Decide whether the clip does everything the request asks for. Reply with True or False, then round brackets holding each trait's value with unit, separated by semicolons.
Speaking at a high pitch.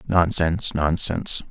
False (85 Hz)